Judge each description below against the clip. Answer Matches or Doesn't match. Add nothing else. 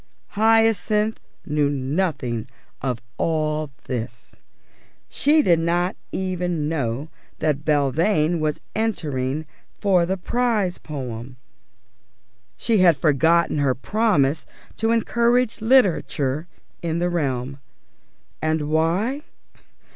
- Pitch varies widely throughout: Matches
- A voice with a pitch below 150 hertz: Doesn't match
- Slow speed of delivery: Matches